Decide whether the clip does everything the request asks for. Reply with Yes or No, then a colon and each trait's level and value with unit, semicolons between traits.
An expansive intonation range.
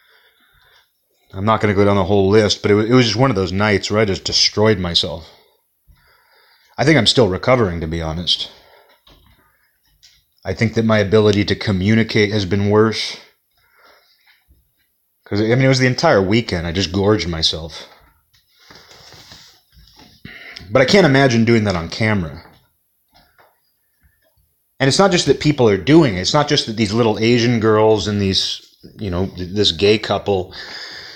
No: average, 3.5 semitones